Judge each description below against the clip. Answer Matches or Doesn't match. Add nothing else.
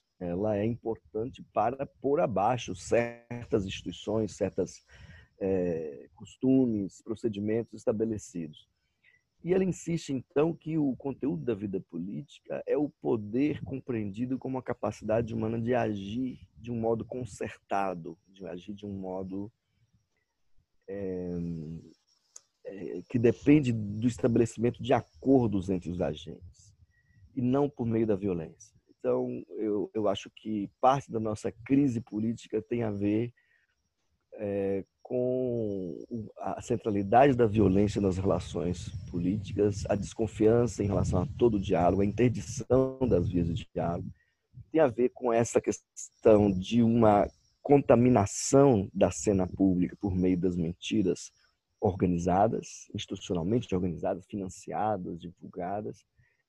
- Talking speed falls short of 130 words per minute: Matches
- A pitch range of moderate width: Matches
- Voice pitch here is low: Matches